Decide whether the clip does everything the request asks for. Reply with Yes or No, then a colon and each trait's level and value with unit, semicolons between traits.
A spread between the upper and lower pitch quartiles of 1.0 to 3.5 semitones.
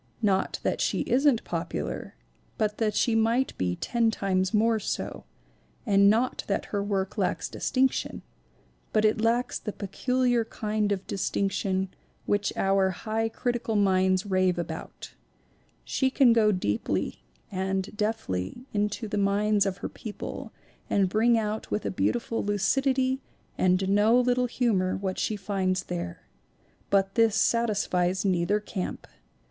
Yes: average, 3.1 semitones